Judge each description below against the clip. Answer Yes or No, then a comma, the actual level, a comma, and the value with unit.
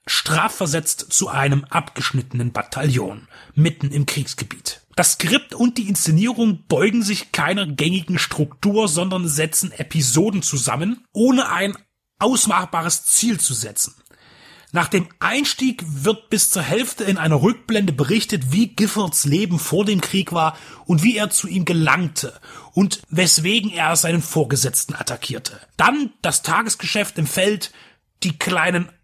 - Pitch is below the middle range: No, medium, 175 Hz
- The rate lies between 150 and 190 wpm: No, average, 135 wpm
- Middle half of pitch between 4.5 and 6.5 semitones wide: Yes, average, 5.2 semitones